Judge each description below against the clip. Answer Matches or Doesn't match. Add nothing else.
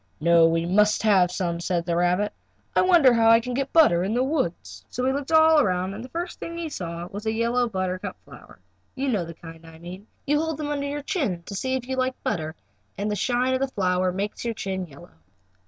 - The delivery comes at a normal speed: Doesn't match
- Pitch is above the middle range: Matches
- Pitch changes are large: Matches